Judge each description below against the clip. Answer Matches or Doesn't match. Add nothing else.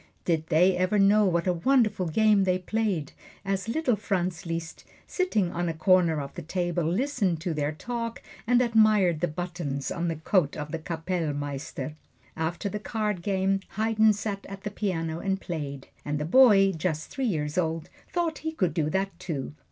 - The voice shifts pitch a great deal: Doesn't match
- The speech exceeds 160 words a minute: Matches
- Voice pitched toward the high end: Doesn't match